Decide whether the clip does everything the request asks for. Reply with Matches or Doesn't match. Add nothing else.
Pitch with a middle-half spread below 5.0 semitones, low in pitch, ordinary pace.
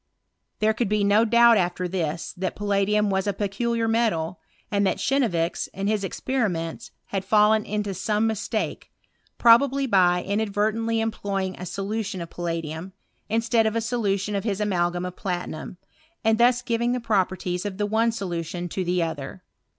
Doesn't match